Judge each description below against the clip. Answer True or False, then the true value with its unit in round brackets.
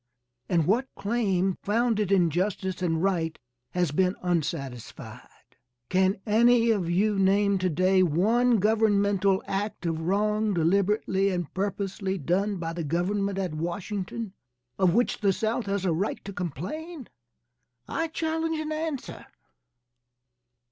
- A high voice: True (195 Hz)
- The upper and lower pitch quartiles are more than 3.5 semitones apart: False (3.2 semitones)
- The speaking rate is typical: False (130 wpm)